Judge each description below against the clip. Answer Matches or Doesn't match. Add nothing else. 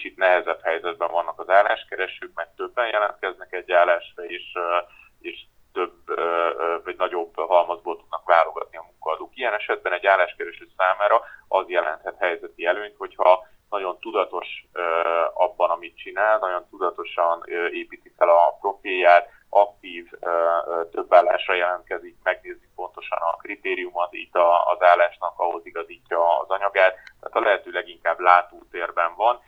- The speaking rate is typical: Matches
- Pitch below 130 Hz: Matches